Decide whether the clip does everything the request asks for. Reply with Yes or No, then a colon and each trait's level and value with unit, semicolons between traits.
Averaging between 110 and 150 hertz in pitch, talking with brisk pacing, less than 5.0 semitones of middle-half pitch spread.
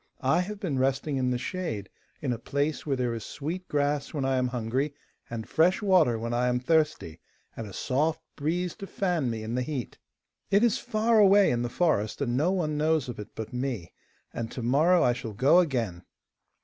No: low, 135 Hz; fast, 210 wpm; average, 5.3 semitones